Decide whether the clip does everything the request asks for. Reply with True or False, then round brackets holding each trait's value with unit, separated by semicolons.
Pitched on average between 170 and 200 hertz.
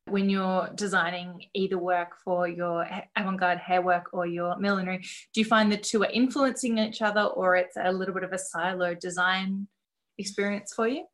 True (190 Hz)